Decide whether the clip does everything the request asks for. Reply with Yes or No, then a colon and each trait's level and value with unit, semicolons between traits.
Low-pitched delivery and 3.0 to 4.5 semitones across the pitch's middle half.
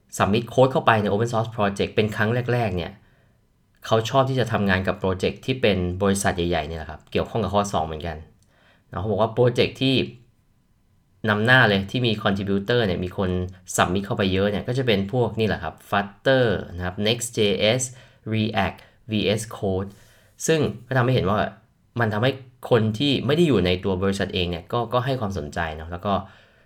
Yes: low, 105 Hz; average, 3.7 semitones